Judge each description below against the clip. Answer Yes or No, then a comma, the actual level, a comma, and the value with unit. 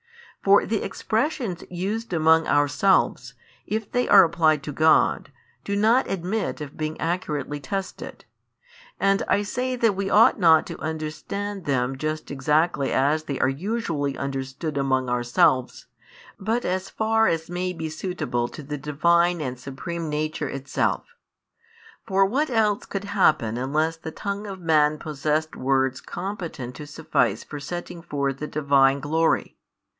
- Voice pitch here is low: No, medium, 160 Hz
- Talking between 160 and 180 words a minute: No, average, 145 wpm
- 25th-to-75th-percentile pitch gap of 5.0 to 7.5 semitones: Yes, wide, 5.4 semitones